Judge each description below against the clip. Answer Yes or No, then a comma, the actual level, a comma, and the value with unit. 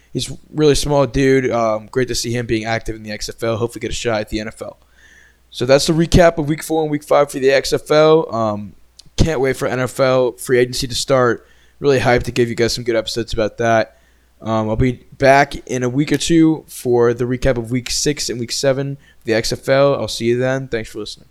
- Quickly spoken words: Yes, fast, 230 wpm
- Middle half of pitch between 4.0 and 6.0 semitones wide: No, average, 3.4 semitones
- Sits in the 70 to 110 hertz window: No, low, 125 Hz